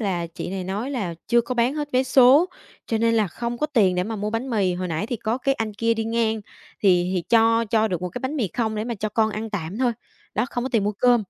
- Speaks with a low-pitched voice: No, high, 225 Hz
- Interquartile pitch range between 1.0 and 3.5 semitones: Yes, average, 3.2 semitones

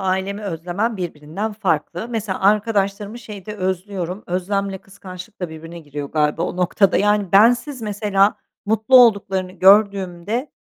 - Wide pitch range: No, average, 2.7 semitones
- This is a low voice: No, high, 195 Hz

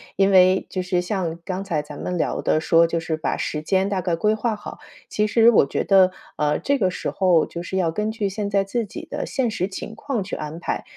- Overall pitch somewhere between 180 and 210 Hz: Yes, high, 190 Hz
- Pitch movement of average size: Yes, average, 3.9 semitones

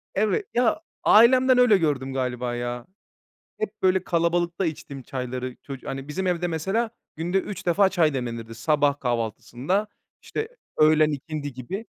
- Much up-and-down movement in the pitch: Yes, wide, 6.8 semitones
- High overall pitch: No, medium, 155 Hz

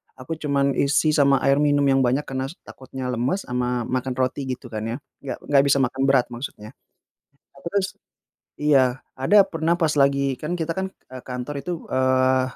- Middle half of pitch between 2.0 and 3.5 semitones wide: Yes, narrow, 2.4 semitones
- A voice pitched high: No, low, 135 Hz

